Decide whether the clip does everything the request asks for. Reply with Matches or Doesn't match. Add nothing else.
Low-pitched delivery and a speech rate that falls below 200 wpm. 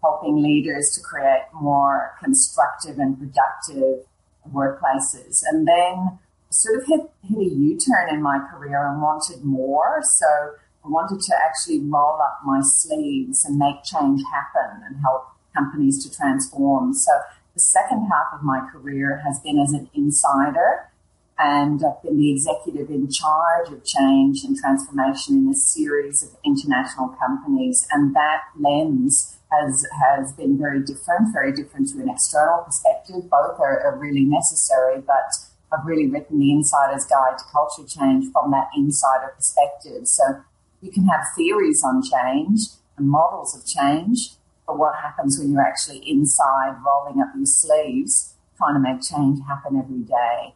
Doesn't match